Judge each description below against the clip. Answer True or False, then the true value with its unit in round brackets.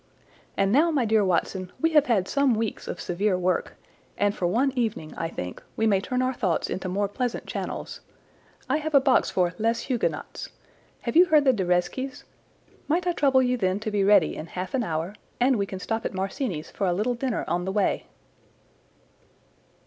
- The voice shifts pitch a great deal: True (5.7 semitones)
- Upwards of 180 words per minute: True (200 wpm)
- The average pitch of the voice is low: False (215 Hz)